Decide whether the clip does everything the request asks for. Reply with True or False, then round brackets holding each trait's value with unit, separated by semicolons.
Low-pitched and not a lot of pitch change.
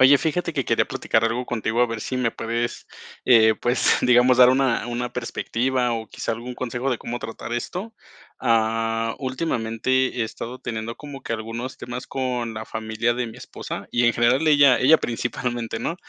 True (120 Hz; 2.2 semitones)